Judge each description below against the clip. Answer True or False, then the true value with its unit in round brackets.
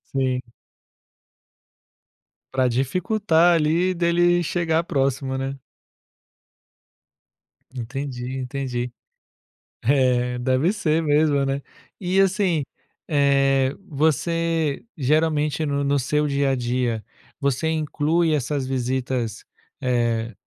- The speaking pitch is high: False (140 Hz)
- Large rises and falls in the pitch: False (3.7 semitones)